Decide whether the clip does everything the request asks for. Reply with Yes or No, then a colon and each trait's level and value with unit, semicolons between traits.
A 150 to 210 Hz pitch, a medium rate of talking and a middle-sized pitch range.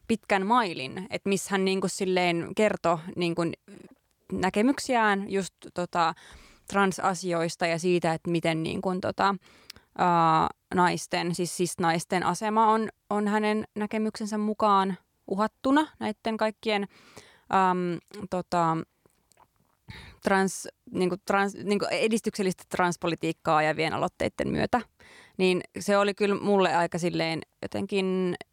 Yes: high, 190 Hz; average, 115 wpm; average, 3.0 semitones